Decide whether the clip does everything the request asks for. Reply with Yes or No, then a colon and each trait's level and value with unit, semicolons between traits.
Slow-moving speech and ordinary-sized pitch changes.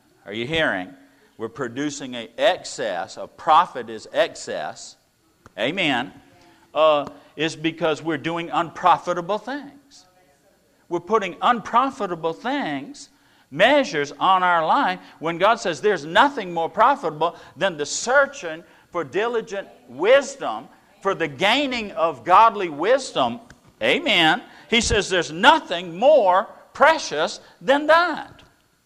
No: slow, 115 wpm; wide, 8.3 semitones